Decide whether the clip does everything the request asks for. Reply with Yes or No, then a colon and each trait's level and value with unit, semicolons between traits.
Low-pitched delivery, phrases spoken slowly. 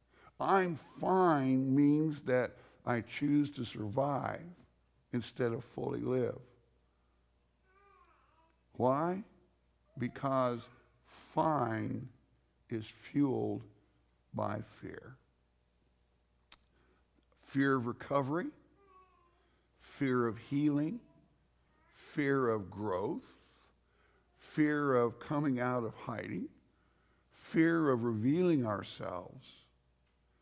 Yes: low, 120 Hz; slow, 75 wpm